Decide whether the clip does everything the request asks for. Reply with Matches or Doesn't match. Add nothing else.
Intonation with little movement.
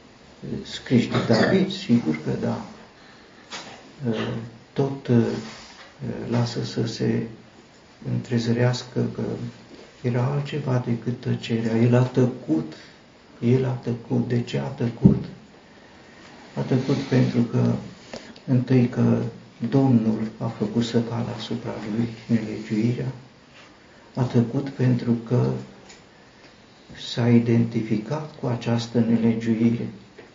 Matches